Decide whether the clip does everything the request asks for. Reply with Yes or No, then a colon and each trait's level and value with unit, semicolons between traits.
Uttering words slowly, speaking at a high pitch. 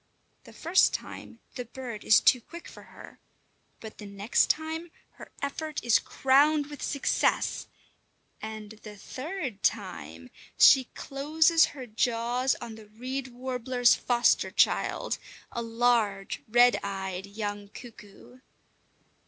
Yes: slow, 125 wpm; high, 240 Hz